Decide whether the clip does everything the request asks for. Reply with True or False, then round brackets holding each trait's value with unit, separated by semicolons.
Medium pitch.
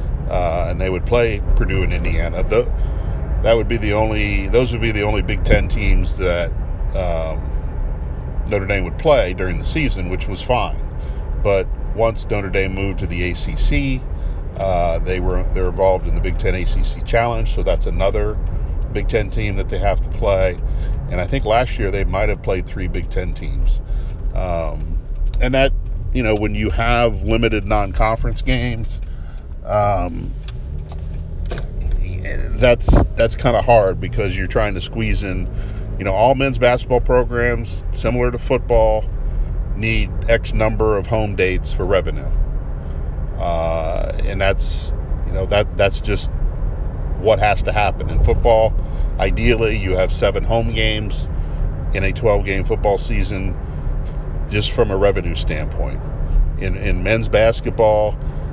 False (95 Hz)